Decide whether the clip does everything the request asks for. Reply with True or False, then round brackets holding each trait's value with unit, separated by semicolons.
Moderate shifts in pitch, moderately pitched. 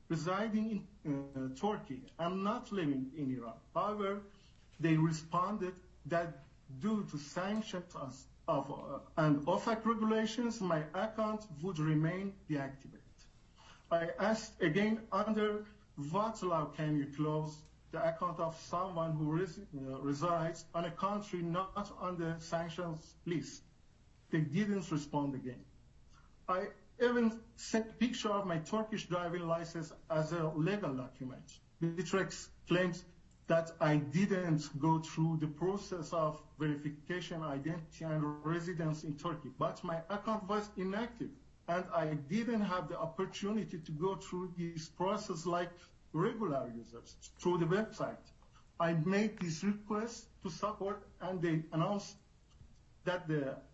True (4.2 semitones; 175 Hz)